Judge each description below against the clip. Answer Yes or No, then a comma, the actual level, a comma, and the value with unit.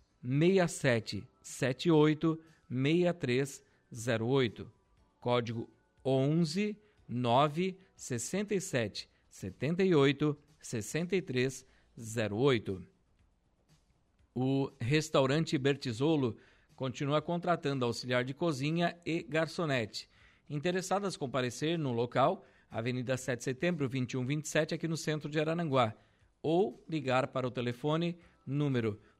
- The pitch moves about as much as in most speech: Yes, average, 4.9 semitones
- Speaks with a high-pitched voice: No, low, 135 Hz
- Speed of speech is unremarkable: No, slow, 110 wpm